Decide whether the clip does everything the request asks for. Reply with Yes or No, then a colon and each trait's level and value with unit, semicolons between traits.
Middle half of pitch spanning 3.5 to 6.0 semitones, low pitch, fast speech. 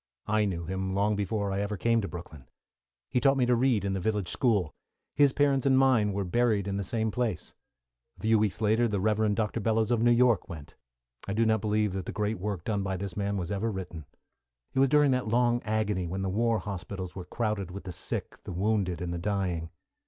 No: average, 3.1 semitones; low, 105 Hz; fast, 230 wpm